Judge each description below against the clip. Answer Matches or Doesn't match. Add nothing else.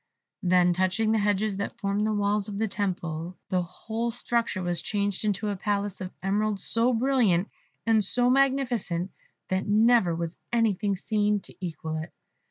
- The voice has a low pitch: Doesn't match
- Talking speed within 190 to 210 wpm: Doesn't match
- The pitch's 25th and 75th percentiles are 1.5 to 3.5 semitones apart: Matches